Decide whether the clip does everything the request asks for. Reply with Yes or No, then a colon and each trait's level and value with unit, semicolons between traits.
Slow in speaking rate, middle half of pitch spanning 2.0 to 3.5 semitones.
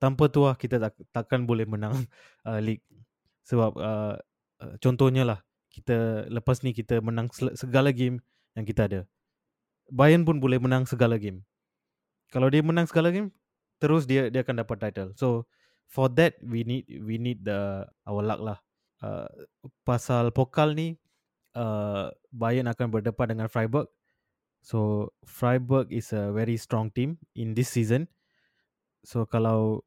No: average, 150 wpm; average, 2.9 semitones